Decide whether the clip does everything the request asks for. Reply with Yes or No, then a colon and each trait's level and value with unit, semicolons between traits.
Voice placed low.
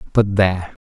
Yes: low, 100 Hz